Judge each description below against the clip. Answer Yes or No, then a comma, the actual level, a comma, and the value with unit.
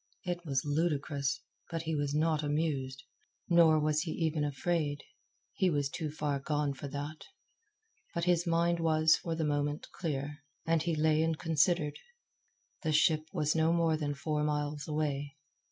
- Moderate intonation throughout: No, narrow, 2.0 semitones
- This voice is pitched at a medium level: Yes, medium, 155 Hz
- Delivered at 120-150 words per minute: No, average, 160 wpm